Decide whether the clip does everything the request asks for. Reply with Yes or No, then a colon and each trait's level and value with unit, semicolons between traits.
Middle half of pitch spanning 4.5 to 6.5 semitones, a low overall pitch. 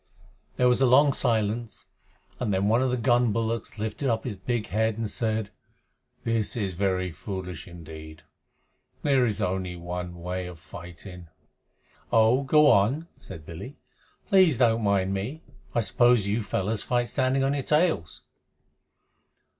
Yes: average, 5.0 semitones; low, 110 Hz